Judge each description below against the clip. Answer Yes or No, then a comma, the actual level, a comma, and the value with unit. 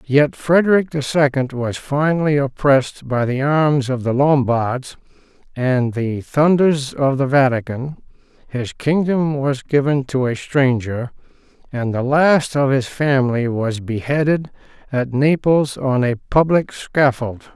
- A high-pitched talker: No, low, 135 Hz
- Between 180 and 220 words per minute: No, slow, 135 wpm